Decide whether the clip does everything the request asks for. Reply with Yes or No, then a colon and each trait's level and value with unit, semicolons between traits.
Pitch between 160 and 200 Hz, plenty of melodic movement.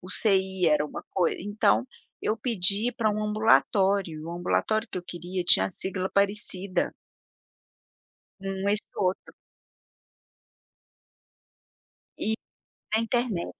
No: high, 195 Hz; average, 2.8 semitones